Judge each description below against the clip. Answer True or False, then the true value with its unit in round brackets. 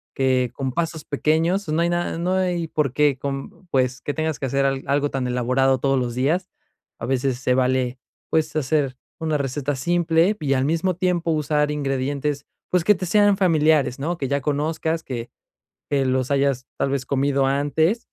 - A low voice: False (145 Hz)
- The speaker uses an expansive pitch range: False (3.5 semitones)